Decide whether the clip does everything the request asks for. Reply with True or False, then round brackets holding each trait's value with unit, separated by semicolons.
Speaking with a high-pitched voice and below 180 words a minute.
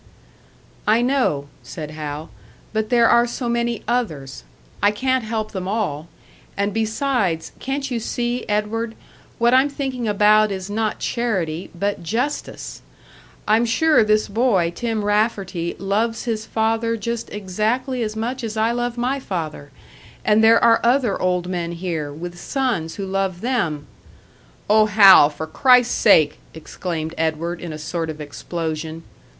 True (215 Hz; 150 wpm)